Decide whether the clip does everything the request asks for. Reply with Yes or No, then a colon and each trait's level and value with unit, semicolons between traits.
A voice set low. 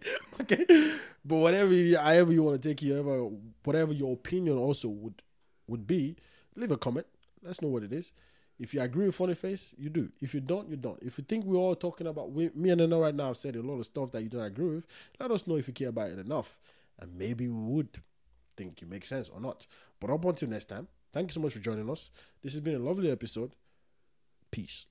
No: medium, 145 Hz